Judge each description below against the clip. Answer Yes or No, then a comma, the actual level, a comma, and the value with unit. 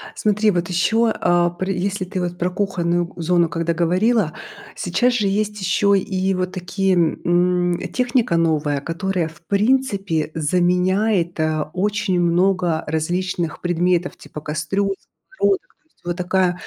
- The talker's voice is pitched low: No, medium, 180 Hz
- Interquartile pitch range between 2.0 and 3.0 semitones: Yes, narrow, 2.5 semitones